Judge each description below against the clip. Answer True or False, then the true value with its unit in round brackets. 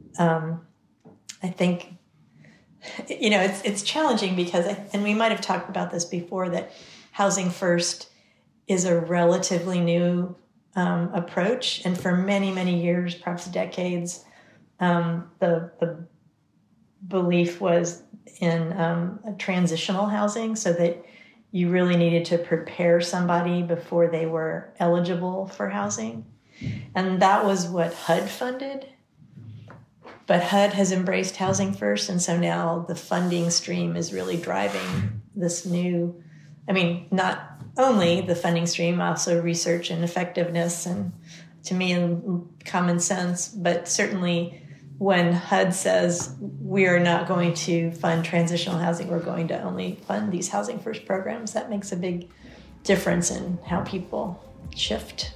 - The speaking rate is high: False (140 wpm)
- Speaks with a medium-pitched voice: True (175 Hz)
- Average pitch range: False (1.9 semitones)